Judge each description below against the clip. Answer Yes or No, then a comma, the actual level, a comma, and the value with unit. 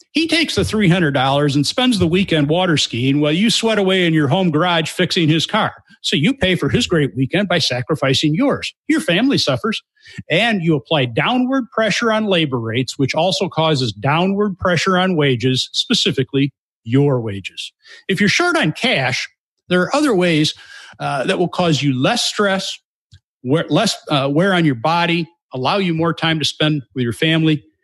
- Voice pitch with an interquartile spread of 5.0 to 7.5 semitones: Yes, wide, 5.6 semitones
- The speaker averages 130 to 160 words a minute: No, average, 180 wpm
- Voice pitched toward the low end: No, medium, 165 Hz